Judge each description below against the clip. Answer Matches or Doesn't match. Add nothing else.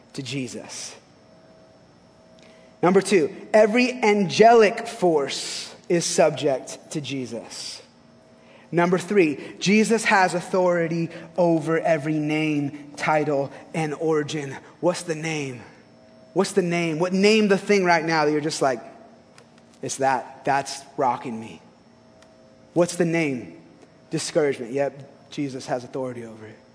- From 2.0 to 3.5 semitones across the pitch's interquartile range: Doesn't match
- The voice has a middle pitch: Matches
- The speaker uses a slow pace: Matches